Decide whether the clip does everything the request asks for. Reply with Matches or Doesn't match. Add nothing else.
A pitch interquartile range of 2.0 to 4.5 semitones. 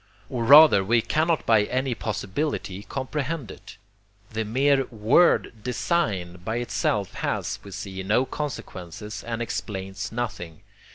Doesn't match